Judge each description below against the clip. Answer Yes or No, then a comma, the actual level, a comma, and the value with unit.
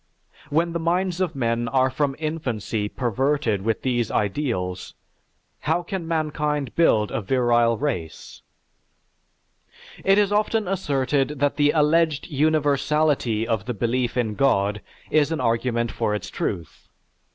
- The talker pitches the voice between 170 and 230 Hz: No, low, 135 Hz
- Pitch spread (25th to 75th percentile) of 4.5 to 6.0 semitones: Yes, average, 5.1 semitones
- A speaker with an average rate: No, slow, 130 wpm